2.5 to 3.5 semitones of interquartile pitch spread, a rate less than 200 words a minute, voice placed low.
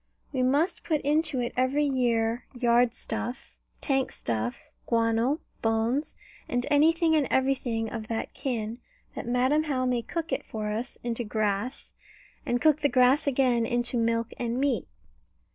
No: average, 3.2 semitones; average, 150 wpm; high, 245 Hz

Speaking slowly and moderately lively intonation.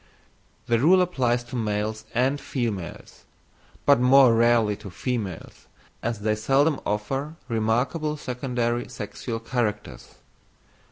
Yes: slow, 110 wpm; average, 3.6 semitones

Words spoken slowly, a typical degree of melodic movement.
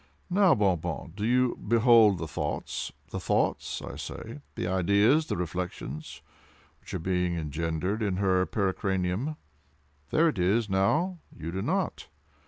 Yes: slow, 120 wpm; average, 4.9 semitones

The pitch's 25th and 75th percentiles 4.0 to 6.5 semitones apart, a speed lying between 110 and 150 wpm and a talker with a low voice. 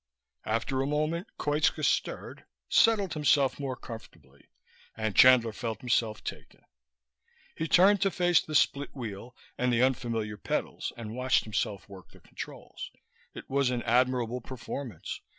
Yes: average, 4.3 semitones; average, 140 wpm; low, 125 Hz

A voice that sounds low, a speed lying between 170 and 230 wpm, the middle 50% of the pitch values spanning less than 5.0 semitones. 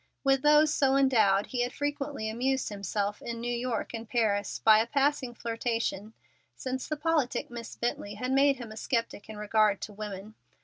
No: high, 235 Hz; average, 180 wpm; average, 3.8 semitones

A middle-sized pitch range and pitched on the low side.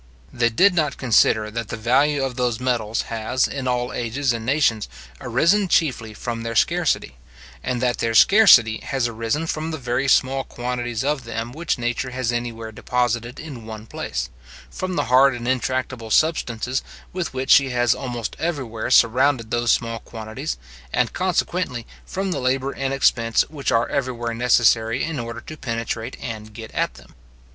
Yes: average, 3.0 semitones; low, 120 Hz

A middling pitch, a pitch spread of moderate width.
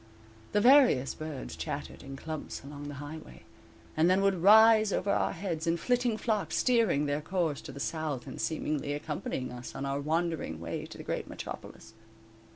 No: medium, 155 Hz; wide, 5.7 semitones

